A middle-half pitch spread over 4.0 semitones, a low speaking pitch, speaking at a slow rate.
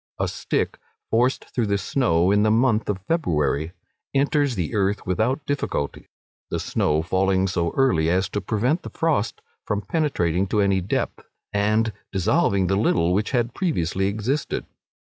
No: average, 5.2 semitones; low, 100 Hz; average, 155 wpm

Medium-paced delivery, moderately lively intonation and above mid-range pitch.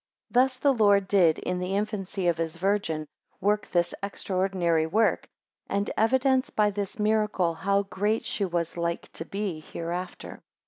Yes: average, 155 wpm; average, 3.3 semitones; high, 195 Hz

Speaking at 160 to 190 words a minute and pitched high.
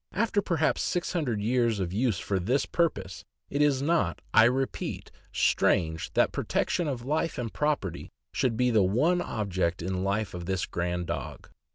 No: average, 170 wpm; low, 115 Hz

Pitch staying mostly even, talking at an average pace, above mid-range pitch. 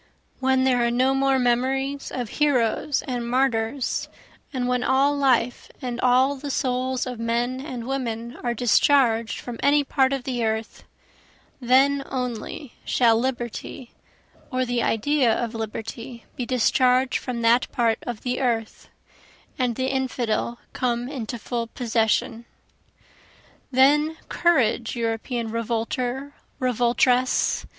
No: narrow, 2.0 semitones; slow, 125 wpm; very high, 250 Hz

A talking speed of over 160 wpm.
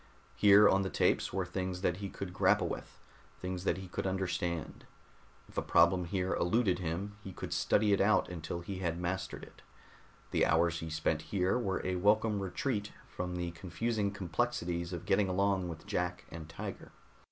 Yes: average, 180 wpm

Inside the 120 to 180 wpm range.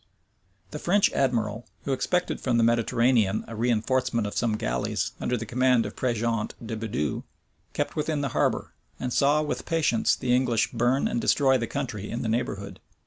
Yes: average, 175 wpm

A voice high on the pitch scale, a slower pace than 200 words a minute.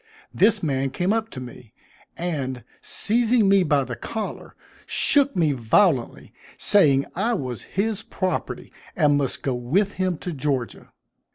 No: medium, 170 Hz; average, 145 wpm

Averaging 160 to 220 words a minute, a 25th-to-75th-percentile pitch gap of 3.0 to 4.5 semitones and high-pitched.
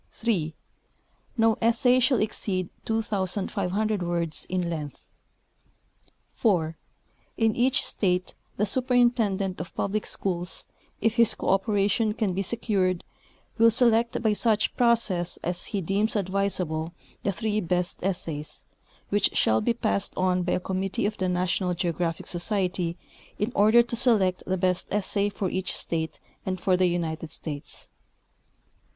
No: slow, 135 wpm; average, 3.6 semitones; high, 195 Hz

